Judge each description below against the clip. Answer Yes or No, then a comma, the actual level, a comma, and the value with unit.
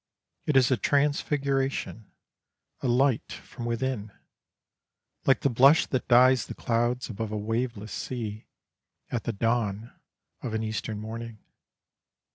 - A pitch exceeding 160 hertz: No, low, 120 Hz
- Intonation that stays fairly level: No, average, 3.0 semitones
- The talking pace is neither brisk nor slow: No, slow, 125 wpm